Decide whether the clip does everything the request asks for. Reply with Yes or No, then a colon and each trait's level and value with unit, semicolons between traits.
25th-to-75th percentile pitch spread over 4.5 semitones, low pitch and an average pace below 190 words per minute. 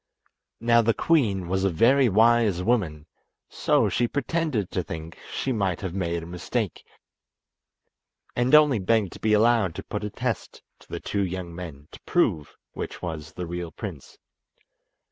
Yes: average, 5.2 semitones; low, 100 Hz; average, 165 wpm